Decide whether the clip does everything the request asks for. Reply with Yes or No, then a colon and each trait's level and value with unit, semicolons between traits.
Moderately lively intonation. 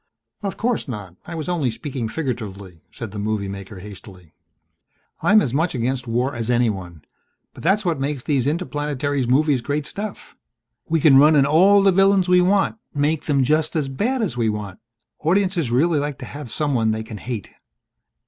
No: wide, 6.3 semitones